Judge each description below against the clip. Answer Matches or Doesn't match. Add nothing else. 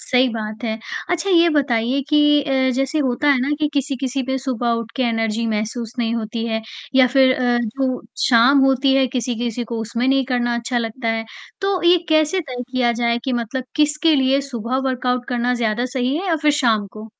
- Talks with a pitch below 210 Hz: Doesn't match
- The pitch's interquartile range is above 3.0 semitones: Doesn't match